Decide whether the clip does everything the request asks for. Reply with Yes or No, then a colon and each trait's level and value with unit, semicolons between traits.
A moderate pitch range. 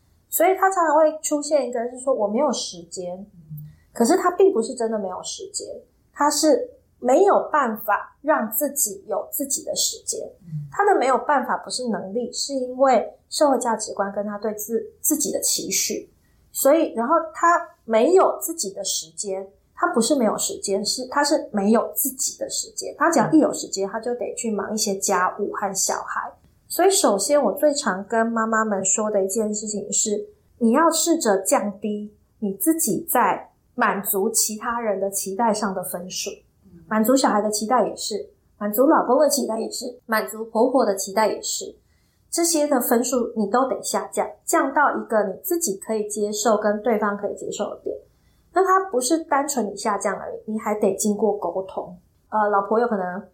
No: wide, 6.4 semitones